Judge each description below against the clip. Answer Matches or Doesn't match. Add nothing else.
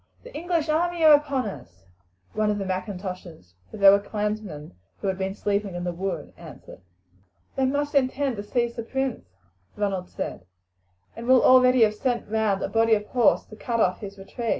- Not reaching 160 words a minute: Doesn't match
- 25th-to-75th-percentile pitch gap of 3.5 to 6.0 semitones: Matches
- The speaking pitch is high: Matches